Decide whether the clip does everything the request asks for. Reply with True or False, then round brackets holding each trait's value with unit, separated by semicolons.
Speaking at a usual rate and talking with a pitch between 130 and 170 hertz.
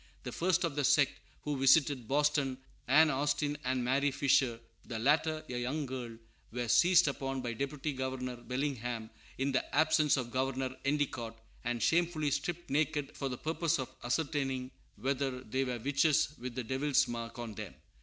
True (165 wpm; 135 Hz)